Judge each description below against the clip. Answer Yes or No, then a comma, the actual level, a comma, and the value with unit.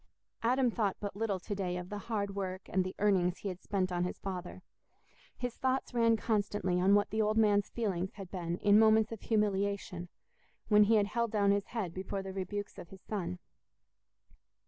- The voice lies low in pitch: No, high, 200 Hz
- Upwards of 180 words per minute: Yes, average, 195 wpm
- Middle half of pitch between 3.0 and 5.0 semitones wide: No, narrow, 2.6 semitones